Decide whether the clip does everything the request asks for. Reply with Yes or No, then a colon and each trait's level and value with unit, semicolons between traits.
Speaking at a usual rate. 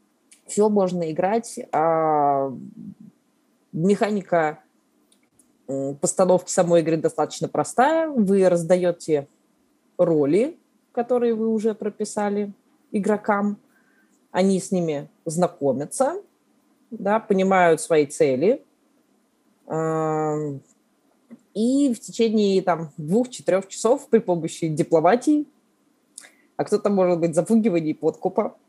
No: slow, 85 wpm